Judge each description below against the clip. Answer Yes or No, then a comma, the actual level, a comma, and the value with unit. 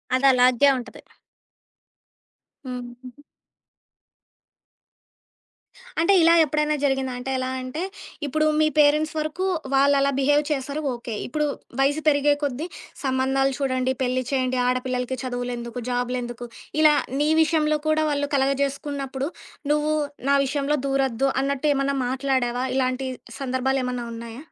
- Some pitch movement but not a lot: No, narrow, 2.3 semitones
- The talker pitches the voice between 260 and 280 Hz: Yes, very high, 270 Hz